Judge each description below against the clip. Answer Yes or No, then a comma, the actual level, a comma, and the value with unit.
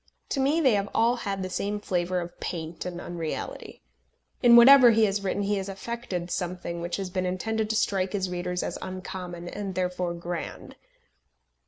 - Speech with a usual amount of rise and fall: Yes, average, 3.0 semitones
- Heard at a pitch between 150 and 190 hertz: Yes, medium, 185 Hz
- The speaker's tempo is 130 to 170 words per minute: No, average, 180 wpm